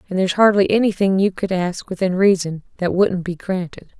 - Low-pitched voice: No, high, 190 Hz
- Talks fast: No, average, 195 wpm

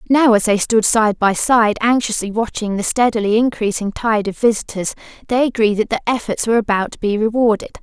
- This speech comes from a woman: Yes, female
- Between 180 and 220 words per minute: Yes, average, 190 wpm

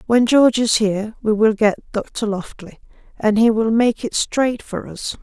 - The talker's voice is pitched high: Yes, high, 220 Hz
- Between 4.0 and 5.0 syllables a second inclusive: Yes, 4.3 syllables/s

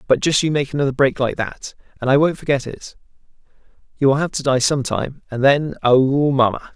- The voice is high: No, low, 135 Hz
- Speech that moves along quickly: No, average, 195 wpm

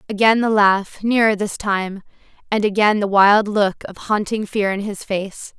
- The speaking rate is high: No, average, 185 wpm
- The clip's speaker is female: Yes, female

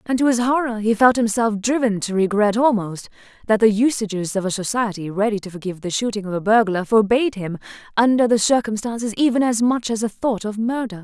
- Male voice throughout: No, female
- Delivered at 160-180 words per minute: No, fast, 205 wpm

